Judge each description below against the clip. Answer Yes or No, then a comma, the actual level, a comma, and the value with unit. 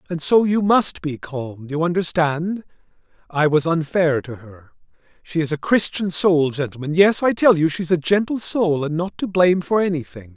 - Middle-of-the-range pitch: Yes, medium, 165 Hz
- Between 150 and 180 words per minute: No, average, 195 wpm